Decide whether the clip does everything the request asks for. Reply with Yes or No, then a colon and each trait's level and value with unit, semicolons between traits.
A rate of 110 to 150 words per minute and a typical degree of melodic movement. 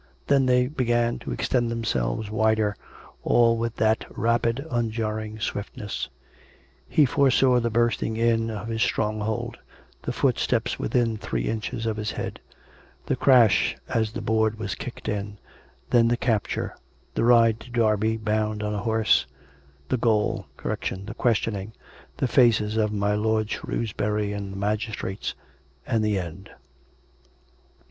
No: average, 140 wpm; narrow, 1.9 semitones